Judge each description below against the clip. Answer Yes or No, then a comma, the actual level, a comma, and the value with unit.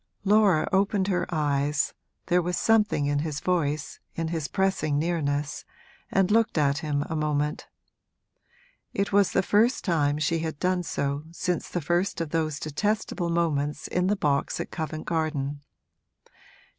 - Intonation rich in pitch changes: No, average, 3.9 semitones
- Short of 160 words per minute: Yes, average, 150 wpm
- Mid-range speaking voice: Yes, medium, 160 Hz